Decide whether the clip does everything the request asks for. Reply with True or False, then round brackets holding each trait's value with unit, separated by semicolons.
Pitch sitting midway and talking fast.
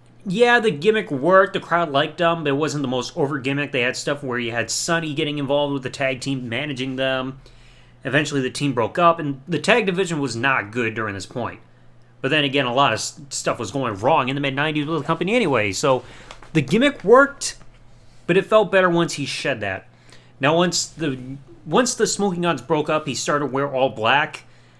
True (145 Hz; 215 wpm)